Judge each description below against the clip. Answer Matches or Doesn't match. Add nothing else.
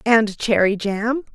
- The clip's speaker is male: Doesn't match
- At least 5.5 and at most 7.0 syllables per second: Doesn't match